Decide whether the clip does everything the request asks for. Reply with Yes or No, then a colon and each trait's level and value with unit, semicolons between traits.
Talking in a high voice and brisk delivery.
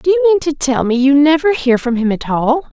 Yes: very high, 285 Hz; fast, 280 wpm